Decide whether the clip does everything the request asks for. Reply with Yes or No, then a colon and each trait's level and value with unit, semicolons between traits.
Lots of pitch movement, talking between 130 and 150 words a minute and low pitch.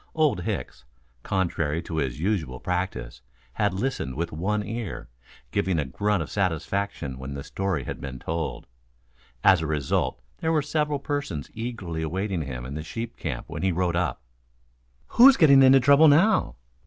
No: wide, 7.6 semitones; average, 165 wpm; very low, 90 Hz